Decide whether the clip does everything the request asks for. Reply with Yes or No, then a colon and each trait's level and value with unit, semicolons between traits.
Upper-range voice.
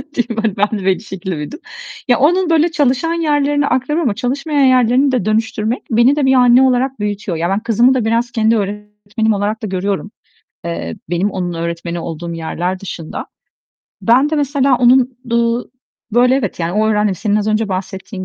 Yes: high, 225 Hz